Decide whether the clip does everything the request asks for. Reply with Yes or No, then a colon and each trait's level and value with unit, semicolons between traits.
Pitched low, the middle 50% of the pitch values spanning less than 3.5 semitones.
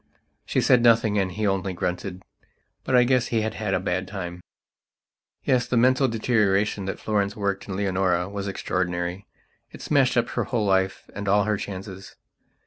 Yes: low, 100 Hz; average, 2.9 semitones